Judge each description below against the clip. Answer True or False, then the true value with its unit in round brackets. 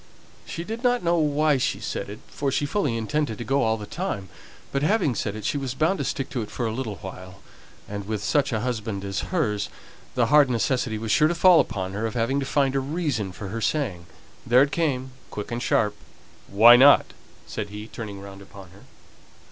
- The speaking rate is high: True (220 wpm)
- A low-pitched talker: True (120 Hz)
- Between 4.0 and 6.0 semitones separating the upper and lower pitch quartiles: True (5.6 semitones)